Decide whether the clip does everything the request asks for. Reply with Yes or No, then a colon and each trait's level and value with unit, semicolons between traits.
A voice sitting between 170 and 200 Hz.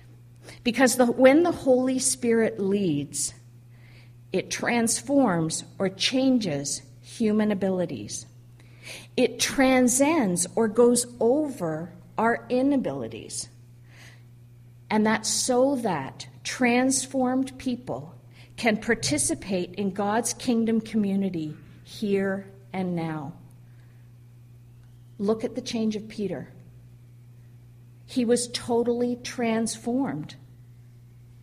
Yes: high, 190 Hz